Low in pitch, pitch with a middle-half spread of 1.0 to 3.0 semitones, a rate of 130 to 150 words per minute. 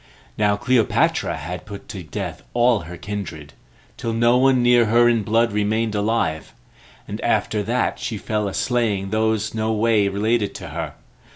No: low, 110 Hz; narrow, 2.4 semitones; average, 165 wpm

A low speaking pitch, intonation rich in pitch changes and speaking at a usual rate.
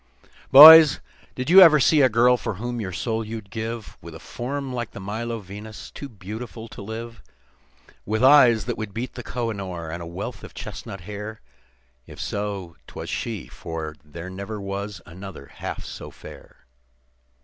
No: low, 110 Hz; average, 3.6 semitones; average, 175 wpm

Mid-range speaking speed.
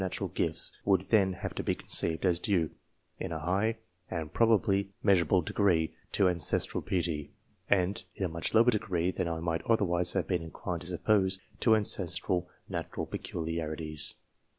Yes: average, 160 wpm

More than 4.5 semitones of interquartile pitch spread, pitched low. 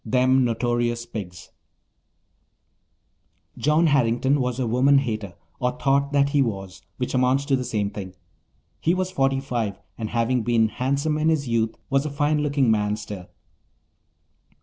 No: average, 3.8 semitones; low, 125 Hz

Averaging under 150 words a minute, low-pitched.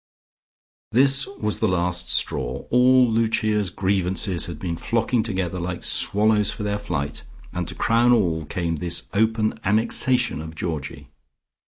Yes: average, 140 wpm; low, 100 Hz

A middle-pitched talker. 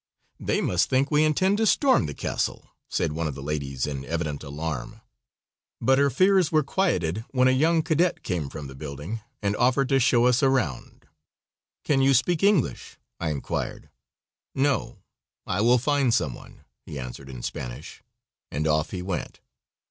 No: low, 115 Hz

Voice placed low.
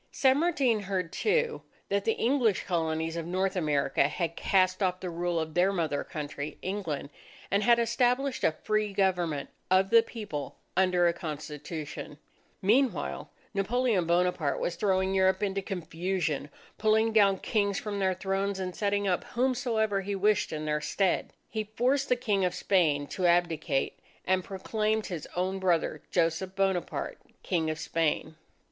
No: high, 190 Hz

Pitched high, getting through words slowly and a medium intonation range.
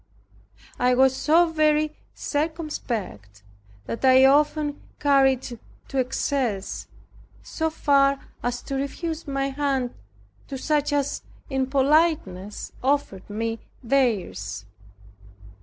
Yes: very high, 270 Hz; slow, 105 wpm; average, 3.4 semitones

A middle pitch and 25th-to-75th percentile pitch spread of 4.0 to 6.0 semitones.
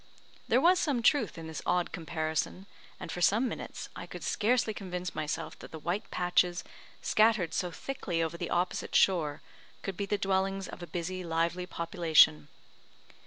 No: medium, 180 Hz; average, 3.2 semitones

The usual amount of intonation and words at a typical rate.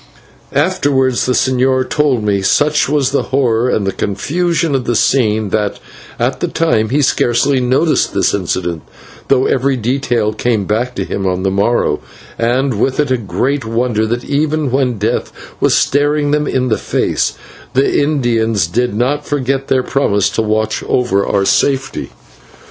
Yes: average, 4.2 semitones; average, 160 wpm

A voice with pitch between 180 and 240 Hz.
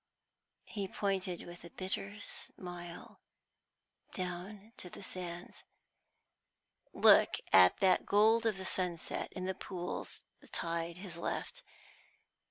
Yes: medium, 185 Hz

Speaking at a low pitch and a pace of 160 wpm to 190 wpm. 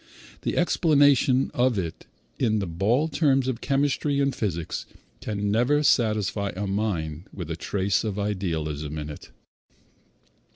No: low, 105 Hz; slow, 135 wpm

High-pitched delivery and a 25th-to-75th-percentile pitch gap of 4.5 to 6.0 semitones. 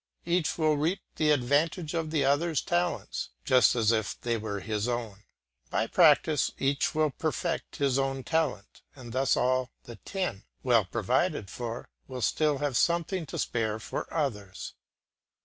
No: low, 135 Hz; average, 5.2 semitones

